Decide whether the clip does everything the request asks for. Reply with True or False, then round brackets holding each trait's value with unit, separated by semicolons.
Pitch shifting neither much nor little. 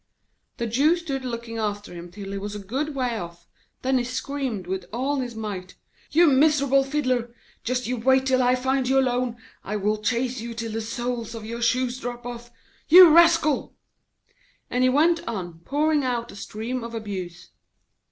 True (3.4 semitones)